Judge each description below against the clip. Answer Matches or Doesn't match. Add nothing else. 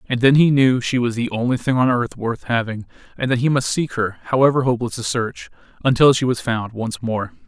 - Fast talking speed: Matches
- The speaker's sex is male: Matches